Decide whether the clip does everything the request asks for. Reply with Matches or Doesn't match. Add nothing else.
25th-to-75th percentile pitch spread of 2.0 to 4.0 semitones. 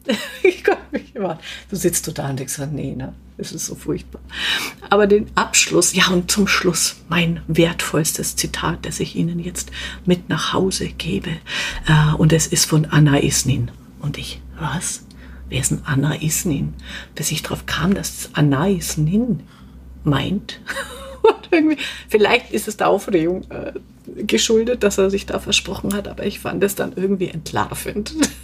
Doesn't match